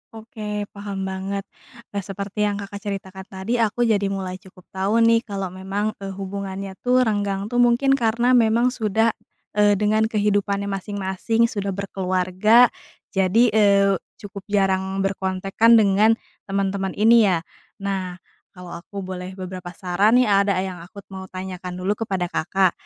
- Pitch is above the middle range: Yes, high, 200 Hz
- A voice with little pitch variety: Yes, narrow, 2.2 semitones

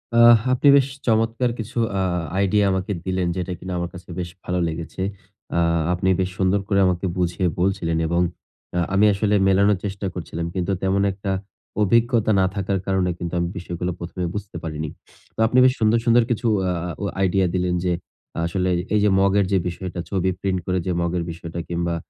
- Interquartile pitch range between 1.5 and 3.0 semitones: Yes, narrow, 2.5 semitones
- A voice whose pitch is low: Yes, very low, 95 Hz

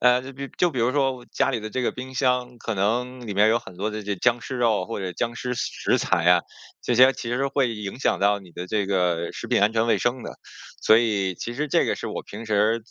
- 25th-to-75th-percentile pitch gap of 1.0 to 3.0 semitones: No, average, 3.6 semitones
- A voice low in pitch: Yes, low, 115 Hz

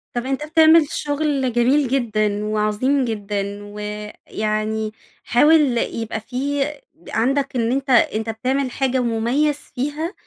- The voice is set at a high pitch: Yes, high, 245 Hz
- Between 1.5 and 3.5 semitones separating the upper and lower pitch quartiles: No, average, 4.5 semitones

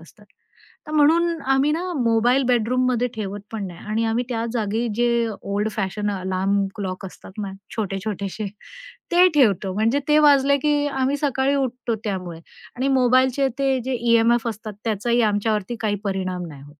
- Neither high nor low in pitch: No, high, 230 Hz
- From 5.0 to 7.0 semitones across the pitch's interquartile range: No, average, 4.6 semitones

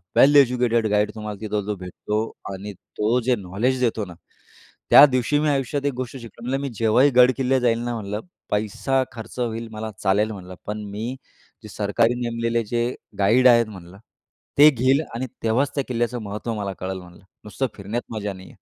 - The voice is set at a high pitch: No, low, 115 Hz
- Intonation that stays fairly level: No, average, 3.4 semitones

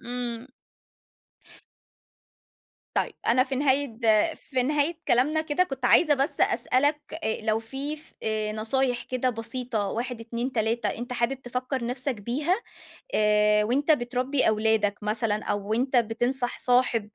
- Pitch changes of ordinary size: Yes, average, 3.0 semitones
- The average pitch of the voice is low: No, high, 245 Hz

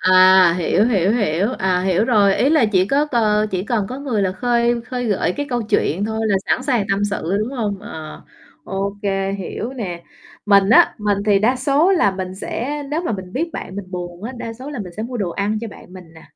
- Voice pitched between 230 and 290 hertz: No, high, 205 Hz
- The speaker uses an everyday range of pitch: Yes, average, 4.3 semitones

